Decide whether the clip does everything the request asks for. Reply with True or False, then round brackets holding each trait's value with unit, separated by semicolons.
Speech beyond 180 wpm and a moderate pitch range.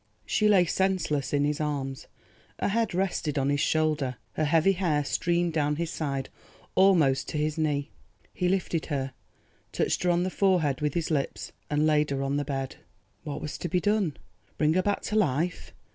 True (190 wpm; 3.7 semitones)